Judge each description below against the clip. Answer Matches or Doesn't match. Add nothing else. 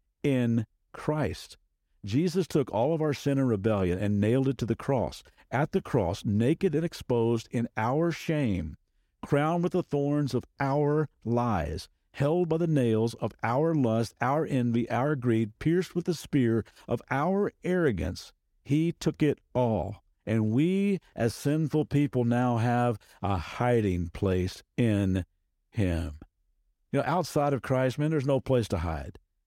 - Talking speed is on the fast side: Doesn't match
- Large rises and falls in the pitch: Matches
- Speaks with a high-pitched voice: Doesn't match